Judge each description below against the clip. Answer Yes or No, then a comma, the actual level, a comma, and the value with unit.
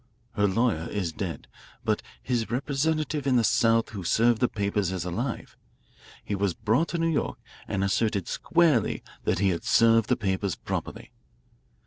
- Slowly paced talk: No, average, 160 wpm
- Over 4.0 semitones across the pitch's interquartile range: Yes, average, 4.4 semitones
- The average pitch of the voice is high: No, low, 110 Hz